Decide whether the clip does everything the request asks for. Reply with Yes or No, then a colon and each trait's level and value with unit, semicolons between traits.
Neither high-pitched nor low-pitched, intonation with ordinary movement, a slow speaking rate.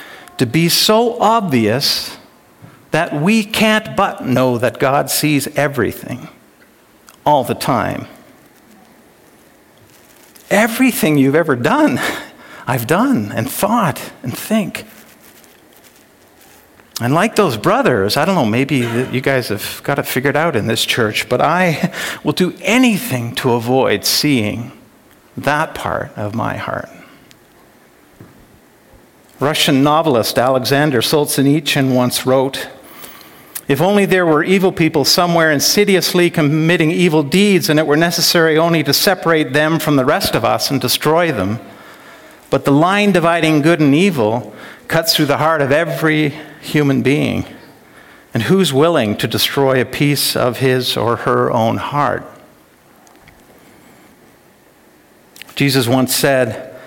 Yes: medium, 150 Hz; average, 4.9 semitones; slow, 130 wpm